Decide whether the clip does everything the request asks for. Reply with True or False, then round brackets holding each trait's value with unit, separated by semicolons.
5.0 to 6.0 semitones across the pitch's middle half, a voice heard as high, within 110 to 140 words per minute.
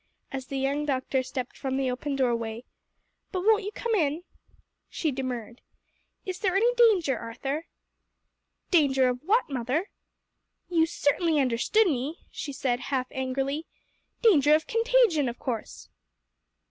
True (5.5 semitones; 280 Hz; 135 wpm)